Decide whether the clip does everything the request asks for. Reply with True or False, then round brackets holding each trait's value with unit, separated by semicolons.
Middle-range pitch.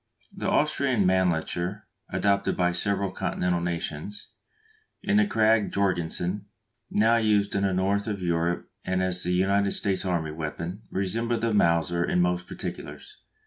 False (95 Hz)